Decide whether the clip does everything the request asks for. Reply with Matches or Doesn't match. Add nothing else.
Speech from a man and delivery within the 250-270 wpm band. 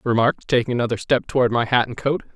Matches